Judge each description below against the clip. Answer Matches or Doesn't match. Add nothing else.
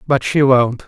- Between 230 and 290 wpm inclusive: Doesn't match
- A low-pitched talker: Matches